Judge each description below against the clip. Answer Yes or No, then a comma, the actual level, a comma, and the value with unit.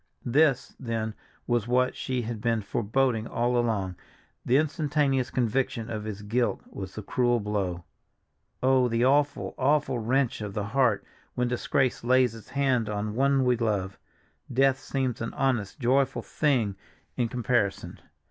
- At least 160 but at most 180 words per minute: No, average, 150 wpm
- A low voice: Yes, low, 120 Hz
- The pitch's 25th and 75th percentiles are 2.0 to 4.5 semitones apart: Yes, average, 3.3 semitones